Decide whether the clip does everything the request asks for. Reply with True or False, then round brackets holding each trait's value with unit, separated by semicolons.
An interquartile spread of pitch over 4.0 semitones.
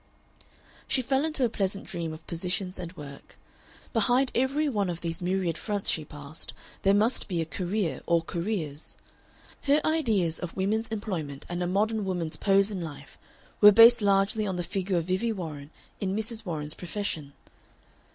True (4.6 semitones)